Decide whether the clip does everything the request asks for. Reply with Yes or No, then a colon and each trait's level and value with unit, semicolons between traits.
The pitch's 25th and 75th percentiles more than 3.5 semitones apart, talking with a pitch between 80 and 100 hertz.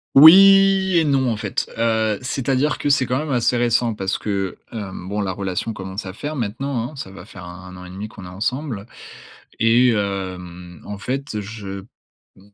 No: average, 5.3 semitones; low, 110 Hz